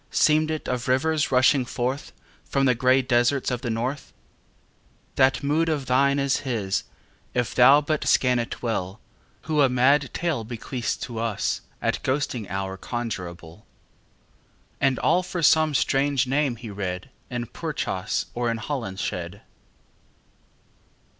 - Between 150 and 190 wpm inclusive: No, average, 140 wpm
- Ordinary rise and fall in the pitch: Yes, average, 3.6 semitones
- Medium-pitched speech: No, low, 125 Hz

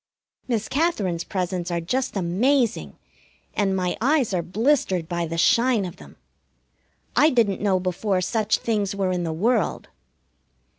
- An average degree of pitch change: Yes, average, 4.7 semitones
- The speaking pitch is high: Yes, high, 195 Hz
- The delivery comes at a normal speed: Yes, average, 145 wpm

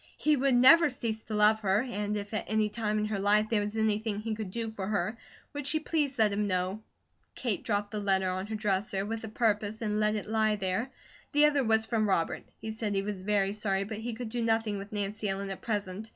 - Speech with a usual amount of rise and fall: No, narrow, 1.7 semitones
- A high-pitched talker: Yes, high, 215 Hz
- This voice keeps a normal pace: No, fast, 240 wpm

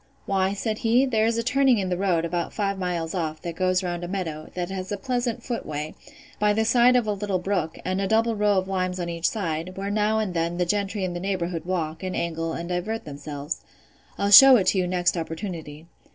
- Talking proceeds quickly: Yes, fast, 225 wpm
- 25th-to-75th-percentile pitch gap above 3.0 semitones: Yes, average, 3.5 semitones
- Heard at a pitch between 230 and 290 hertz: No, medium, 185 Hz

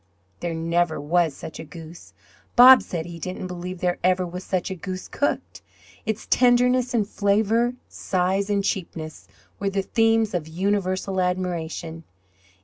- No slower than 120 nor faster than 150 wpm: Yes, average, 145 wpm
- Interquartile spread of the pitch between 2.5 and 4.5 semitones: Yes, average, 3.1 semitones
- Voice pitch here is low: No, medium, 185 Hz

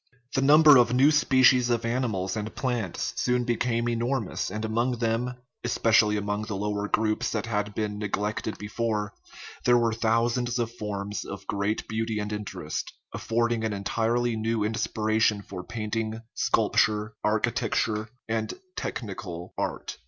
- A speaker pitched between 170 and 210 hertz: No, low, 110 Hz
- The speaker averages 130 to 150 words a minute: Yes, average, 145 wpm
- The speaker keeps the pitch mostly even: Yes, narrow, 2.2 semitones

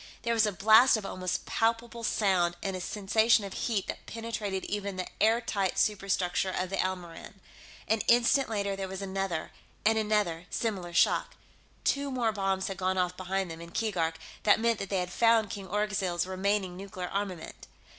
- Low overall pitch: No, high, 195 Hz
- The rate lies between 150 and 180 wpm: Yes, average, 175 wpm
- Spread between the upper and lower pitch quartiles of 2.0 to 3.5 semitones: Yes, average, 2.9 semitones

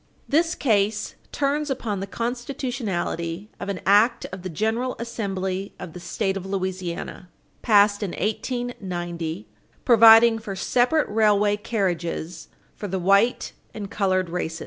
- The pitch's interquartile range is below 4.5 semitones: Yes, average, 3.8 semitones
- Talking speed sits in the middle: No, slow, 130 wpm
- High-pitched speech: Yes, high, 205 Hz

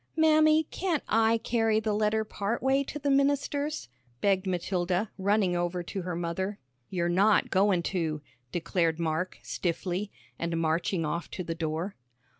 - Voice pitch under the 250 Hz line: Yes, high, 190 Hz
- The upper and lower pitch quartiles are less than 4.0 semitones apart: No, average, 4.5 semitones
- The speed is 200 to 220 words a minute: No, average, 150 wpm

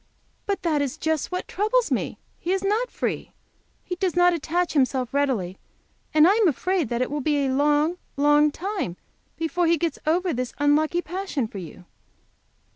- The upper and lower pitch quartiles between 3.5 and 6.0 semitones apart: Yes, average, 4.2 semitones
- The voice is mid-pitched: No, very high, 315 Hz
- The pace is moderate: Yes, average, 180 wpm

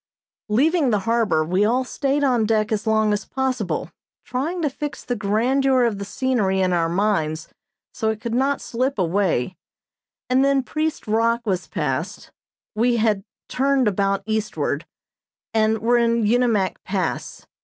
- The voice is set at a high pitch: Yes, high, 220 Hz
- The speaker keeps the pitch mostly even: No, average, 4.3 semitones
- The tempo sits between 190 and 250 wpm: No, average, 155 wpm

